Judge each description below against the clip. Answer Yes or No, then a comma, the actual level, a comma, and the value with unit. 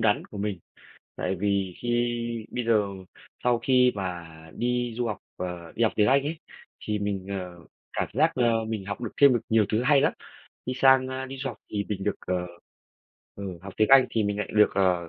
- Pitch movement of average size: Yes, average, 4.0 semitones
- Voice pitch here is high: No, low, 105 Hz